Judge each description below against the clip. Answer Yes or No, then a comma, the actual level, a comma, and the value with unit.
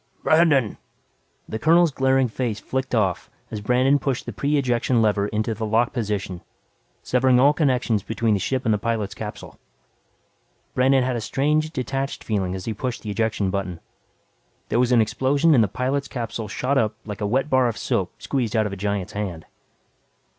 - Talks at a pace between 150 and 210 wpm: Yes, average, 185 wpm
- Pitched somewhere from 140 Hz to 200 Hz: No, low, 115 Hz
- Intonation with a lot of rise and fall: No, average, 4.0 semitones